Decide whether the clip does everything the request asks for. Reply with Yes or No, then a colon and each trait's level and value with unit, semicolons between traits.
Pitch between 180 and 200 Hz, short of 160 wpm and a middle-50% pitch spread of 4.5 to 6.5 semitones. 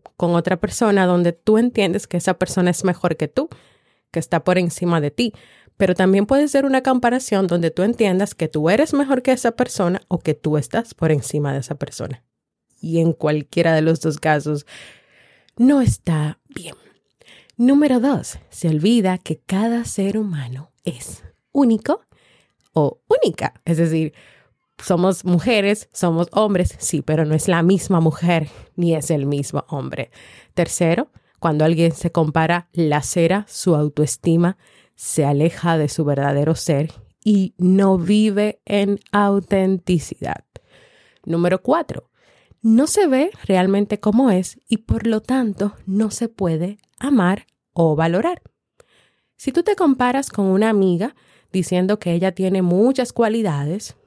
Yes: medium, 185 Hz; average, 150 wpm; average, 4.8 semitones